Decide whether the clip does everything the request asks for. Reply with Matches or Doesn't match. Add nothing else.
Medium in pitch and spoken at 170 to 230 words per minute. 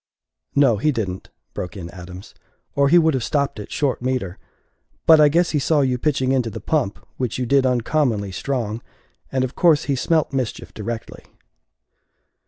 Doesn't match